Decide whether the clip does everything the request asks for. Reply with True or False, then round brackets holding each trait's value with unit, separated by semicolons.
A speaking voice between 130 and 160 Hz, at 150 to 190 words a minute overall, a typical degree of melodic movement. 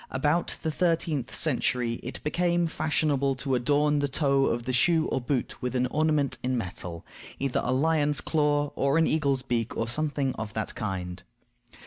True (140 Hz; 170 wpm; 3.7 semitones)